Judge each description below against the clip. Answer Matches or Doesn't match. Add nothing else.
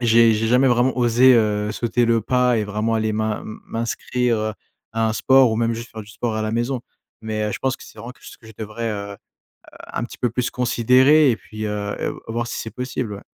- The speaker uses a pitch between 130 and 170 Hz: Doesn't match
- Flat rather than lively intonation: Matches